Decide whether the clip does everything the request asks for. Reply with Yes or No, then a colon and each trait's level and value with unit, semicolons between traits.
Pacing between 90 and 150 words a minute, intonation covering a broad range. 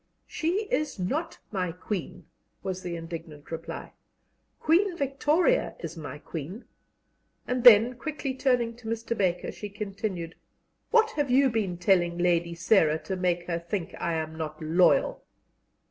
Yes: average, 145 wpm; wide, 6.9 semitones